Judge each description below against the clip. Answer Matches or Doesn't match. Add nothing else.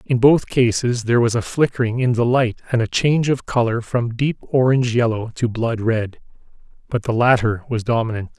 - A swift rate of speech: Doesn't match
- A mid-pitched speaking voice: Doesn't match